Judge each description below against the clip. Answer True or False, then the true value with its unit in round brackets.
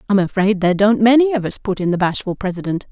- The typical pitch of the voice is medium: False (200 Hz)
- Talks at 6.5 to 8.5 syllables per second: True (6.6 syllables/s)